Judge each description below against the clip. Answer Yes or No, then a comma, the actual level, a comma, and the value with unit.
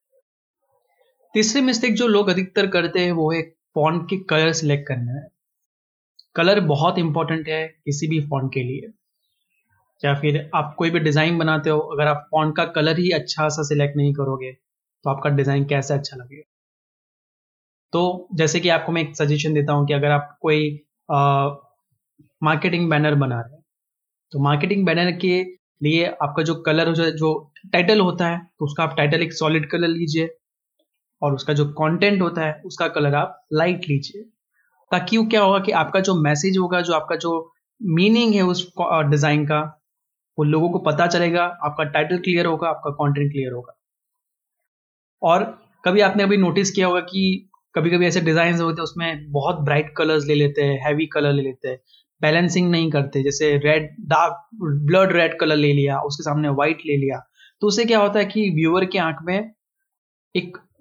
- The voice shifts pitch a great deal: No, average, 3.4 semitones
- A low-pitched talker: No, medium, 160 Hz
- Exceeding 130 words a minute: Yes, average, 180 wpm